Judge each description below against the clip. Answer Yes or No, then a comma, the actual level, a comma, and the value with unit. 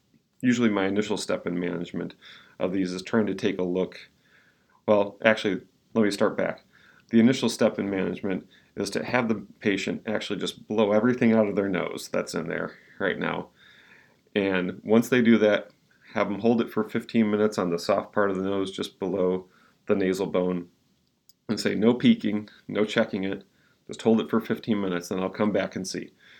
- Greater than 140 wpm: Yes, average, 195 wpm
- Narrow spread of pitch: No, average, 3.2 semitones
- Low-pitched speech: Yes, low, 100 Hz